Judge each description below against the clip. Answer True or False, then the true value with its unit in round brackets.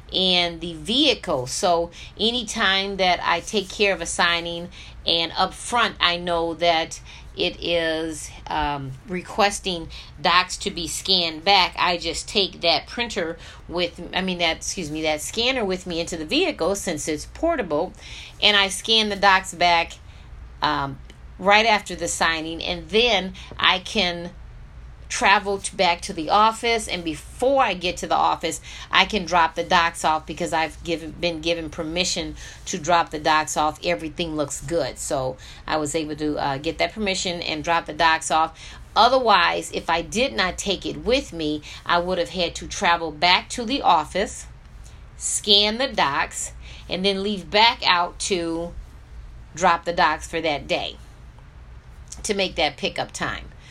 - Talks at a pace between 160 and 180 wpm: True (165 wpm)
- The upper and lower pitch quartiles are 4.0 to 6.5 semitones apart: False (3.3 semitones)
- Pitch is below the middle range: False (170 Hz)